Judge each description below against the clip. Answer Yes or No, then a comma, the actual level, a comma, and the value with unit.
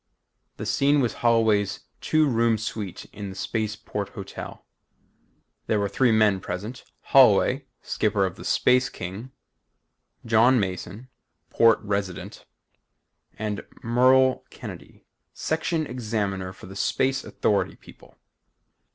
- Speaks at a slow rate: Yes, slow, 115 wpm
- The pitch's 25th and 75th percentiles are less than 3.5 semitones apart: No, average, 3.9 semitones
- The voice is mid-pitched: No, low, 110 Hz